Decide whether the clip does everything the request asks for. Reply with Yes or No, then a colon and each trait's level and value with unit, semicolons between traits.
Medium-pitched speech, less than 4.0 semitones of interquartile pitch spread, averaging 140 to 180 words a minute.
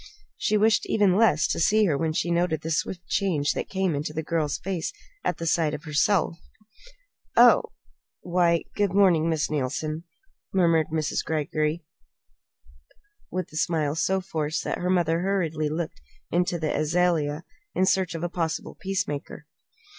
Yes: medium, 165 Hz; average, 3.0 semitones; average, 155 wpm